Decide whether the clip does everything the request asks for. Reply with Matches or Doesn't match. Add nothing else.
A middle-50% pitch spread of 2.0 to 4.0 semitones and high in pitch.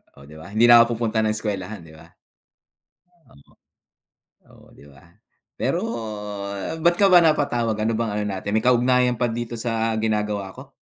Doesn't match